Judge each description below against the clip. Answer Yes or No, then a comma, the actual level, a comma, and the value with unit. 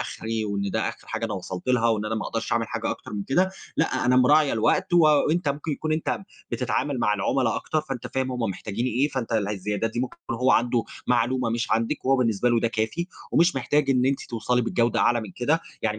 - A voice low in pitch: Yes, low, 120 Hz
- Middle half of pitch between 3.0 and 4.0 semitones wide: Yes, average, 3.4 semitones